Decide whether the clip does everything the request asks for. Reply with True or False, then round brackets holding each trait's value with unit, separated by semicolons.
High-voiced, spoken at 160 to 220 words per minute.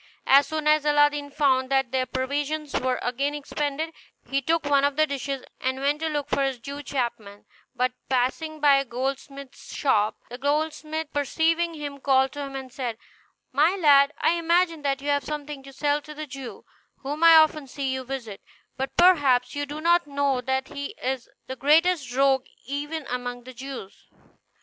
True (280 Hz; 185 wpm)